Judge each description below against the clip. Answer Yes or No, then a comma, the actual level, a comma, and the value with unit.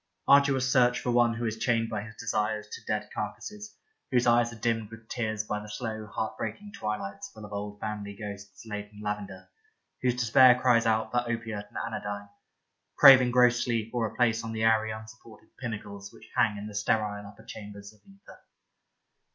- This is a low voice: Yes, low, 110 Hz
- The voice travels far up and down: No, narrow, 2.4 semitones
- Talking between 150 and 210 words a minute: Yes, average, 190 wpm